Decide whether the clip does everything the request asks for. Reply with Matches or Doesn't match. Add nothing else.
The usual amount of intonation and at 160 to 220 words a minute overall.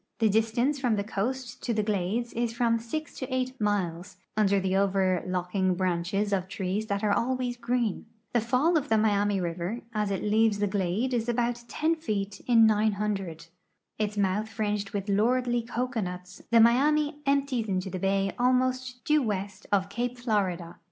Matches